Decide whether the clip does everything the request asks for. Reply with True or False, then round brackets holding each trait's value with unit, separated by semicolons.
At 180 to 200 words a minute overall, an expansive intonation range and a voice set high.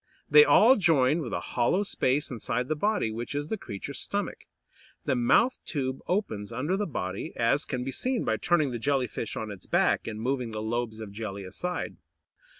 False (195 wpm; 6.4 semitones; 125 Hz)